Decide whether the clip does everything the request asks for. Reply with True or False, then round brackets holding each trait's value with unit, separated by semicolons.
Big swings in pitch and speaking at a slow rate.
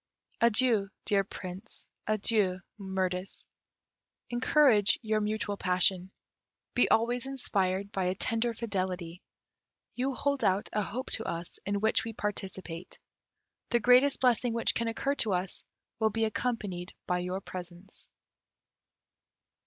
False (3.8 semitones; 125 wpm)